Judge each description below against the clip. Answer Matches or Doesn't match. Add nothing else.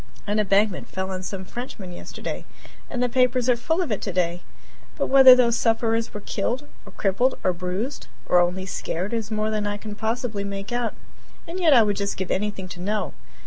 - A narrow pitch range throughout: Doesn't match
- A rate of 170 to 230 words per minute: Matches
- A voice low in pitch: Doesn't match